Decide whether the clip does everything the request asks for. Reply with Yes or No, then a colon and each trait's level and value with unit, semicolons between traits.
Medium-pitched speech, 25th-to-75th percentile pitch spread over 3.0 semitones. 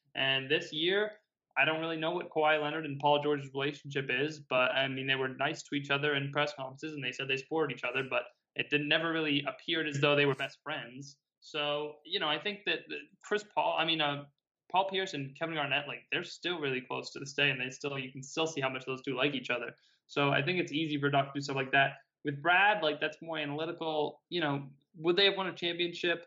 No: medium, 150 Hz; narrow, 2.6 semitones